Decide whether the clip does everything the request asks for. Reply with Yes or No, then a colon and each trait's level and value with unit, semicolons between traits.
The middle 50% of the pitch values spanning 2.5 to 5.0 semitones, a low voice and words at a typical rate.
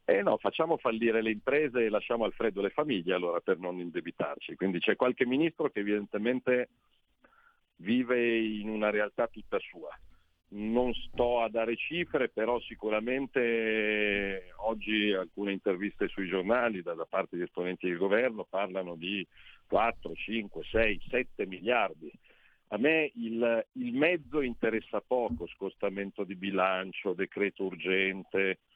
Yes: average, 3.5 semitones; low, 105 Hz; average, 140 wpm